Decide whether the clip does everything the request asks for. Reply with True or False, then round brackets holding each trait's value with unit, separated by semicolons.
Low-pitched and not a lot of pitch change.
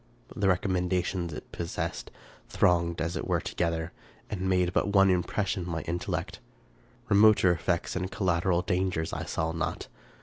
True (90 Hz; 1.8 semitones)